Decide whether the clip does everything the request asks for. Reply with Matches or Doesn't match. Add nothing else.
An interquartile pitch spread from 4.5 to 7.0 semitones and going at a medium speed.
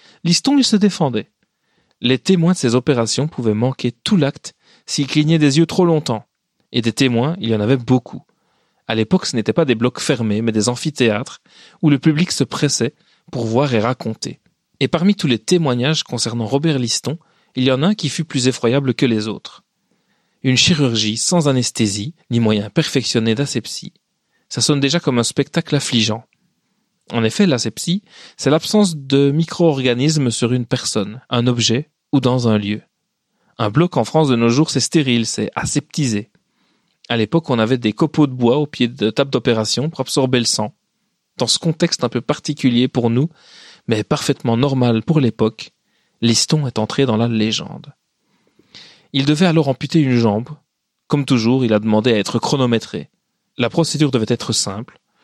Matches